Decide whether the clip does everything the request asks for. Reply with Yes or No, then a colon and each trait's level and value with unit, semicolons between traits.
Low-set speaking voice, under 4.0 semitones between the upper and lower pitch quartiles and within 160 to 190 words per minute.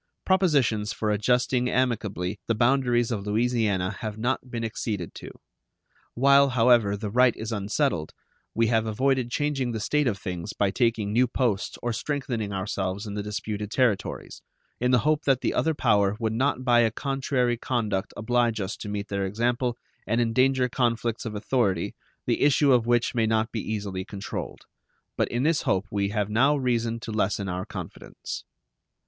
Yes: low, 115 Hz; average, 3.3 semitones; average, 170 wpm